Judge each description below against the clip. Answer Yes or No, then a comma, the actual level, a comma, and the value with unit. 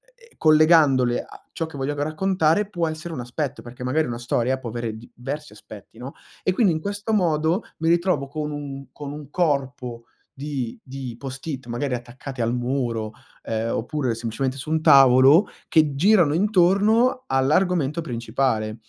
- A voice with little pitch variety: No, average, 4.6 semitones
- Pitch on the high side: No, medium, 140 Hz